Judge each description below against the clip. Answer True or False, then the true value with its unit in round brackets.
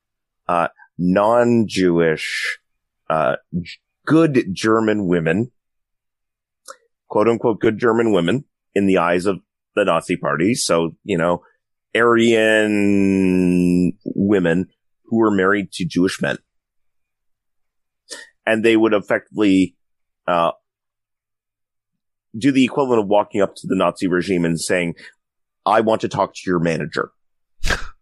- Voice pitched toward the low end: True (100 Hz)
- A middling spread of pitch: True (3.8 semitones)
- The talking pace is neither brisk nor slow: False (115 wpm)